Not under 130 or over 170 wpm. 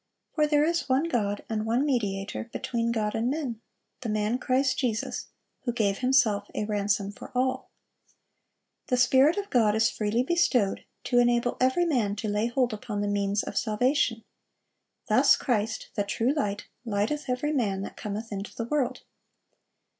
Yes: average, 165 wpm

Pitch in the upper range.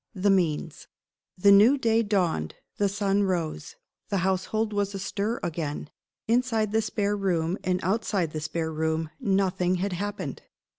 Yes: high, 195 Hz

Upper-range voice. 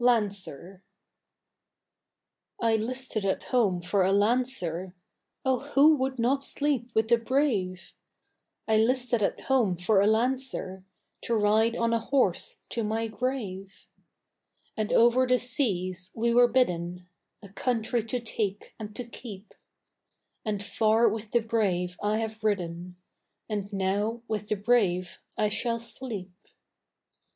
Yes: high, 220 Hz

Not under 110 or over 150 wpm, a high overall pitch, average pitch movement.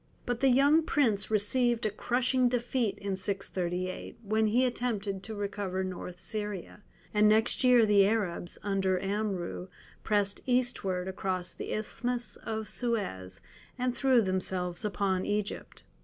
Yes: slow, 135 wpm; high, 210 Hz; average, 4.1 semitones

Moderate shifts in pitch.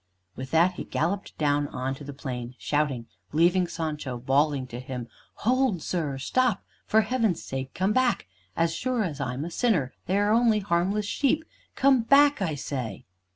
No: wide, 7.9 semitones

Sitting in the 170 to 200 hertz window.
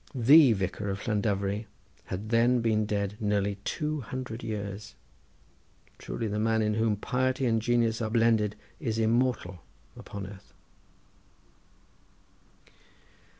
No: low, 110 Hz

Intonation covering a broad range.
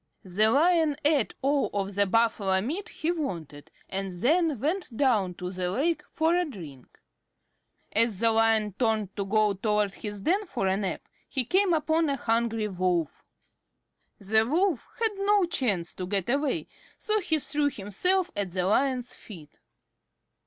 Yes: wide, 8.0 semitones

